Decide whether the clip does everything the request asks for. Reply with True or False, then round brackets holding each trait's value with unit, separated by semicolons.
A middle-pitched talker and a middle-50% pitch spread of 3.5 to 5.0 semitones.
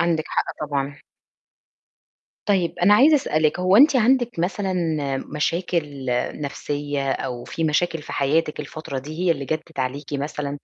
True (155 Hz; 3.8 semitones)